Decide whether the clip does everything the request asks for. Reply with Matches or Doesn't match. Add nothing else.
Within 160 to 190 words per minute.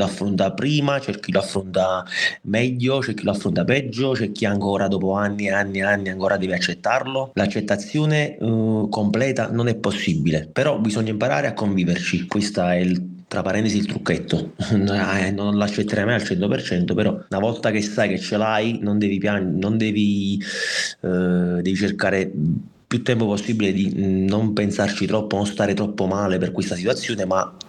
Matches